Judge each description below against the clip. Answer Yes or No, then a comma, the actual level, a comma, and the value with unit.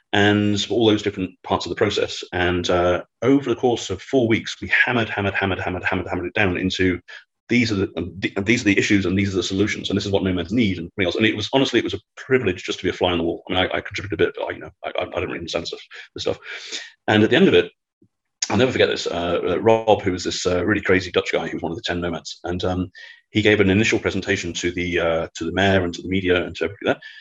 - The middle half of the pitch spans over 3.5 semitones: No, average, 3.2 semitones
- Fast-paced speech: Yes, fast, 290 wpm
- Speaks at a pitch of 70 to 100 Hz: Yes, very low, 95 Hz